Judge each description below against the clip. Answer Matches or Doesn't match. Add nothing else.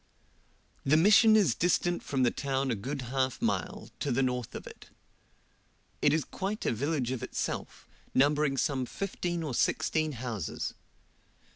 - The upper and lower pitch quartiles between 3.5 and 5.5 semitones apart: Matches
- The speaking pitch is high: Doesn't match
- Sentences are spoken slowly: Doesn't match